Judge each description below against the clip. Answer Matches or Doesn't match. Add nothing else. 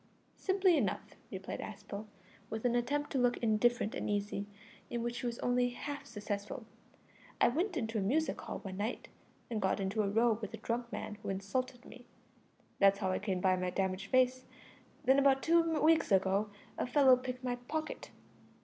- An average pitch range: Matches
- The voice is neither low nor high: Doesn't match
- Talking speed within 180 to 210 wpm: Matches